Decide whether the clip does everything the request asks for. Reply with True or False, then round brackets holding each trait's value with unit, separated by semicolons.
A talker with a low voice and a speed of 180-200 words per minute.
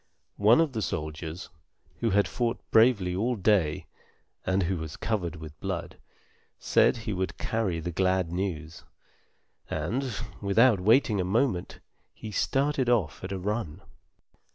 False (100 Hz; 140 wpm)